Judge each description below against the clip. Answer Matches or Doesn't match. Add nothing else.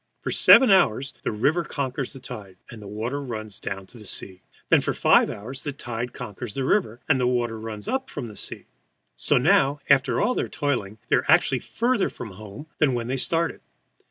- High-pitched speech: Doesn't match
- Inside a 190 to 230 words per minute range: Matches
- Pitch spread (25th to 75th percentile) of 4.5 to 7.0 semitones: Matches